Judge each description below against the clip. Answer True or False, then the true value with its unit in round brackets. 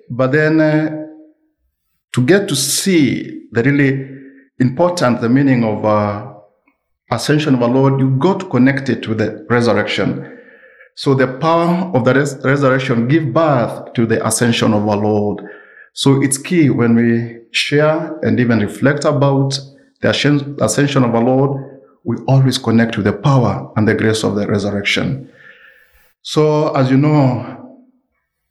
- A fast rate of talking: False (155 wpm)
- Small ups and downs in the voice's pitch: False (4.1 semitones)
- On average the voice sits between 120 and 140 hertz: True (135 Hz)